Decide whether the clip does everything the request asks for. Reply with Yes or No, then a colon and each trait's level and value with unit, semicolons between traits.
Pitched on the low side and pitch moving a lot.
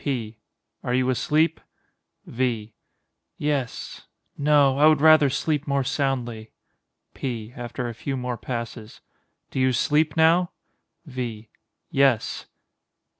No: low, 130 Hz; average, 3.6 semitones